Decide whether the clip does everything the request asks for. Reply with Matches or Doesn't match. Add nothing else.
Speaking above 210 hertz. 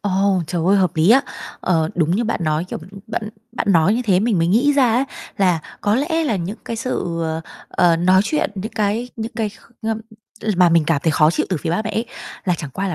Doesn't match